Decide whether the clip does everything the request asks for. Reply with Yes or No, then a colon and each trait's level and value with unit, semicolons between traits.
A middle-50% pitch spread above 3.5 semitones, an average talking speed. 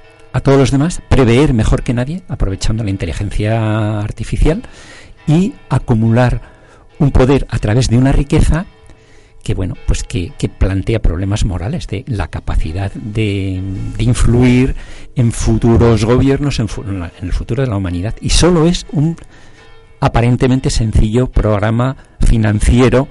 Yes: average, 4.1 semitones; average, 140 wpm